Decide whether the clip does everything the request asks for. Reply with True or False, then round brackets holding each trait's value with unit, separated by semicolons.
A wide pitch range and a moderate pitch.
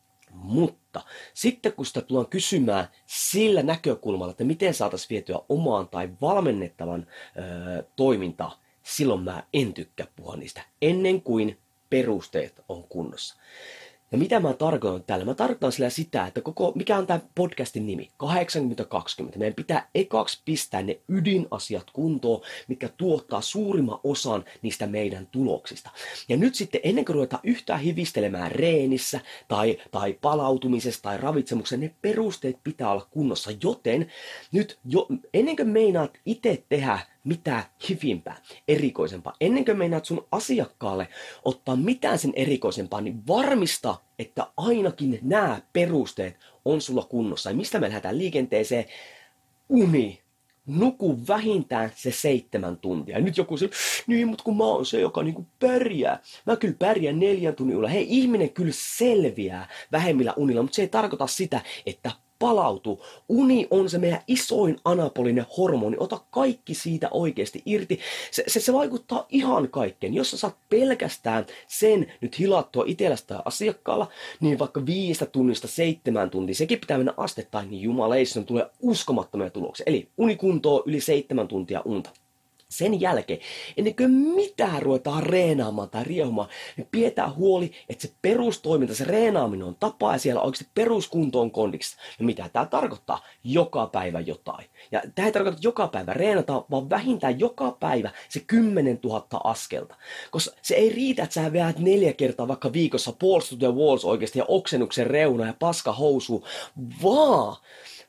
True (8.5 semitones; 155 Hz)